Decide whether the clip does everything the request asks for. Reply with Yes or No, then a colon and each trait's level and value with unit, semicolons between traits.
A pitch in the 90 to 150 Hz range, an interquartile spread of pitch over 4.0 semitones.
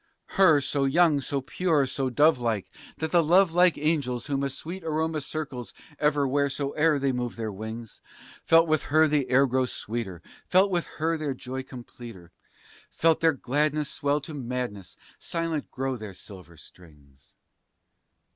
Yes: medium, 140 Hz; average, 4.4 semitones